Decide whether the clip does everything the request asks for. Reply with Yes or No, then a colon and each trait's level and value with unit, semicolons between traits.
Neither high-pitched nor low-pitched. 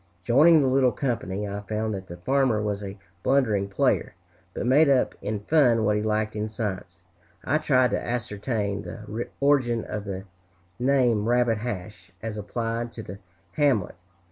No: low, 110 Hz